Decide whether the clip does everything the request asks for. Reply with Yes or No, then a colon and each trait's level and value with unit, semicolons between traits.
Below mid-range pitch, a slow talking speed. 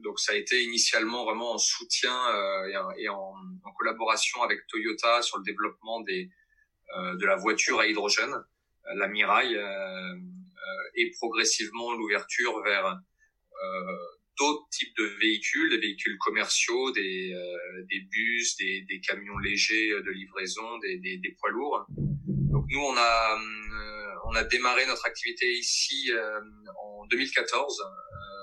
Yes: low, 115 Hz; slow, 130 wpm